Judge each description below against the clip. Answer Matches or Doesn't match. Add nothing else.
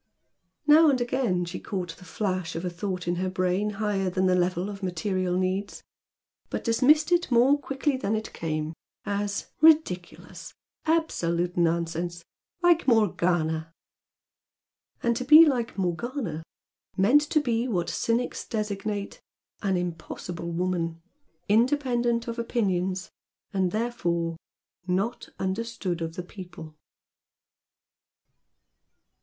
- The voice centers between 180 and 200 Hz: Matches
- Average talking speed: Doesn't match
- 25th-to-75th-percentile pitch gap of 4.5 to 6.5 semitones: Matches